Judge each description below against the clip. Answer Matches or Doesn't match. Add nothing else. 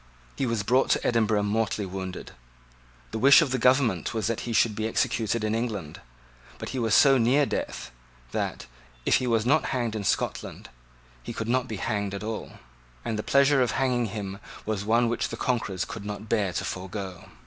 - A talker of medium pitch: Doesn't match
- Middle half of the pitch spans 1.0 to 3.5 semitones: Matches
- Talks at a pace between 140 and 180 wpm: Doesn't match